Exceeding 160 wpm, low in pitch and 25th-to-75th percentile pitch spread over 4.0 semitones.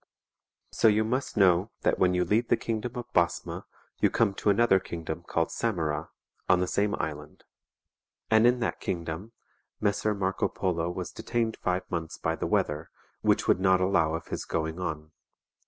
Yes: average, 170 wpm; very low, 95 Hz; average, 4.5 semitones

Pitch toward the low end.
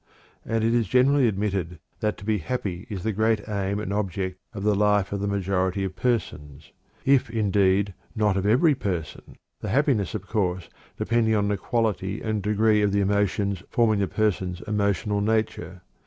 Yes: low, 100 Hz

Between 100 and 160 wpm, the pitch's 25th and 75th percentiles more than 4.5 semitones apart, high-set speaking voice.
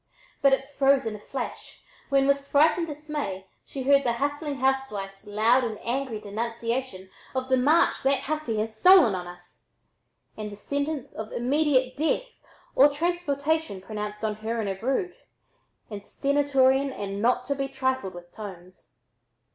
Yes: average, 155 wpm; average, 4.9 semitones; very high, 260 Hz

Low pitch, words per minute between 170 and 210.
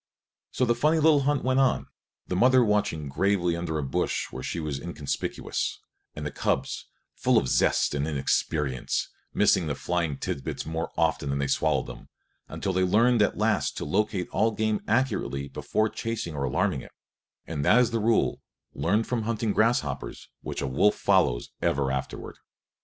Yes: very low, 95 Hz; average, 175 wpm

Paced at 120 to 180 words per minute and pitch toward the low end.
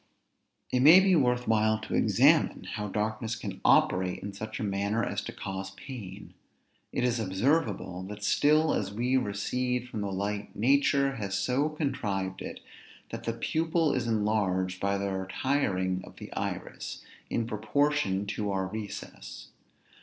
Yes: average, 155 wpm; low, 110 Hz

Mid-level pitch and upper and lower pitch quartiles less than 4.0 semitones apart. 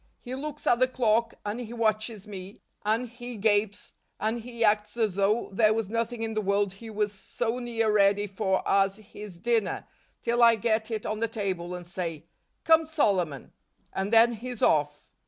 No: high, 215 Hz; average, 2.7 semitones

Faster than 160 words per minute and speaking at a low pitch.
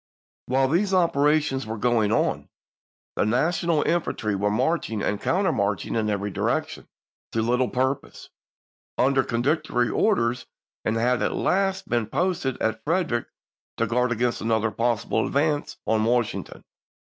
No: average, 140 wpm; low, 125 Hz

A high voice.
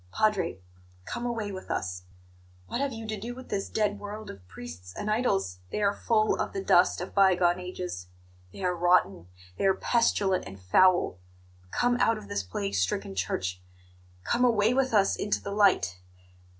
Yes: high, 195 Hz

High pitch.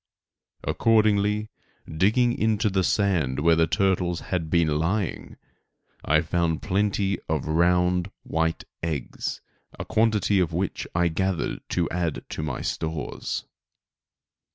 No: very low, 90 Hz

